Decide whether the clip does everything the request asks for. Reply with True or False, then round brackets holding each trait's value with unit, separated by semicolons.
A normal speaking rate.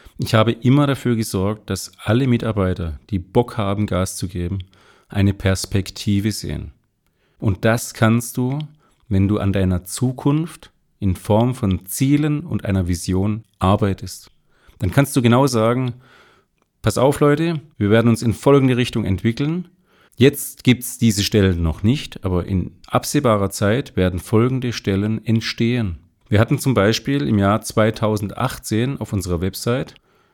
True (145 wpm)